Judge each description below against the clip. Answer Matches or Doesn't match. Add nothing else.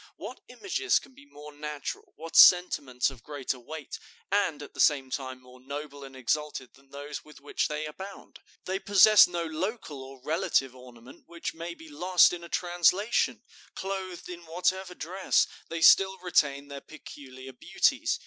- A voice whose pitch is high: Doesn't match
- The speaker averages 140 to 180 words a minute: Matches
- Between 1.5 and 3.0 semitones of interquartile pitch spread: Doesn't match